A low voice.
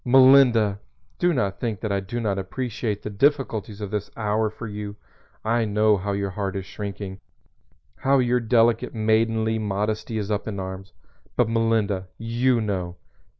Yes: low, 110 Hz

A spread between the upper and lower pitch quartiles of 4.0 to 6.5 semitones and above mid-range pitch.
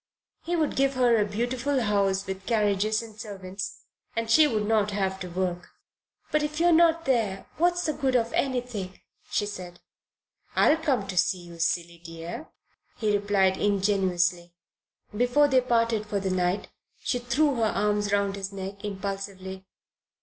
Yes: average, 4.5 semitones; high, 205 Hz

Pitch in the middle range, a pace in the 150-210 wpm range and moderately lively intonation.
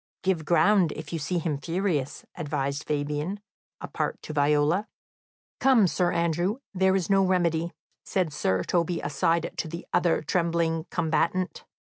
No: medium, 170 Hz; average, 140 wpm; average, 3.2 semitones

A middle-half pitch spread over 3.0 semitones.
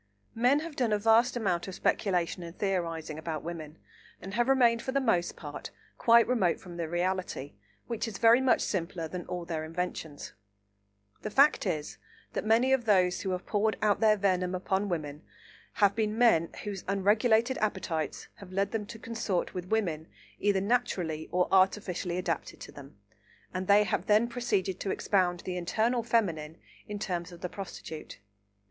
Yes: average, 4.2 semitones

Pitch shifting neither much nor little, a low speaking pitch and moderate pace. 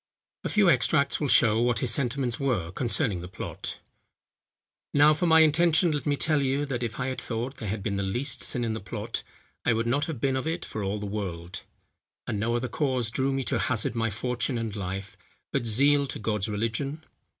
No: average, 4.6 semitones; low, 120 Hz; fast, 215 wpm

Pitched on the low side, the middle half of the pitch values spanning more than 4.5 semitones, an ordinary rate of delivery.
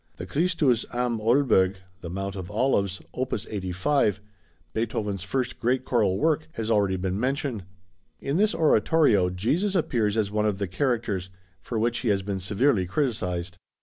Yes: low, 110 Hz; average, 5.2 semitones; average, 155 wpm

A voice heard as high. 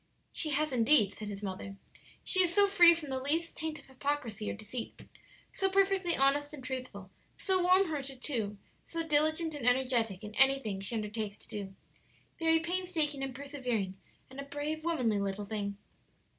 Yes: very high, 270 Hz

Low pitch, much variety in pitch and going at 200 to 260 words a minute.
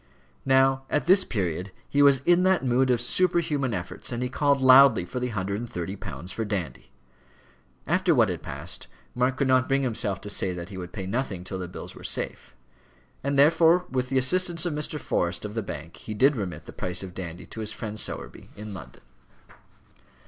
Yes: low, 125 Hz; wide, 6.4 semitones; fast, 205 wpm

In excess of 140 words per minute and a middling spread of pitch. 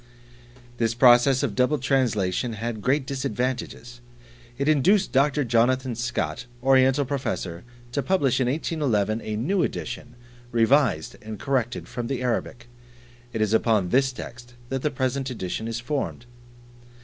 No: slow, 135 wpm; average, 3.0 semitones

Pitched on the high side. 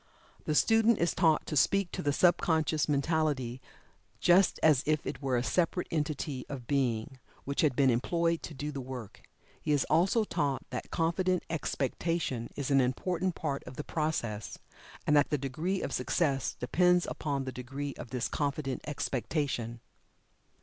No: medium, 145 Hz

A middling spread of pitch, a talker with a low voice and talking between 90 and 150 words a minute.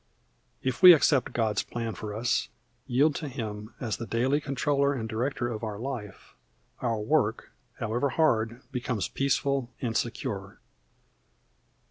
Yes: average, 3.7 semitones; low, 120 Hz; slow, 135 wpm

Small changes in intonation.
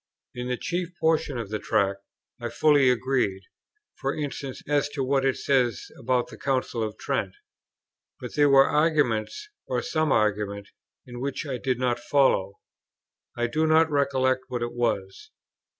No: average, 3.3 semitones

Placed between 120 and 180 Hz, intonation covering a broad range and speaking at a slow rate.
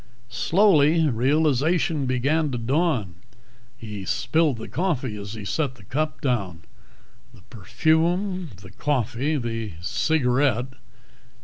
Yes: low, 135 Hz; wide, 5.7 semitones; slow, 110 wpm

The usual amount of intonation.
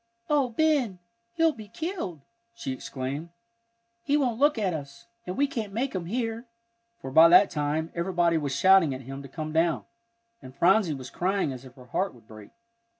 No: wide, 8.3 semitones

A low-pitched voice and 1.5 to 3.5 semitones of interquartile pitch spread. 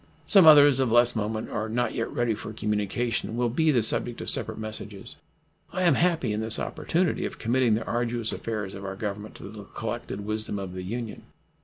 Yes: low, 115 Hz; narrow, 2.5 semitones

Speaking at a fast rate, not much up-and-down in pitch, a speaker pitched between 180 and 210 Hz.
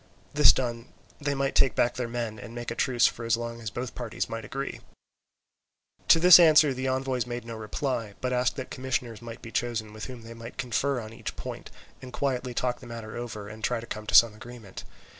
No: fast, 220 wpm; narrow, 2.2 semitones; low, 120 Hz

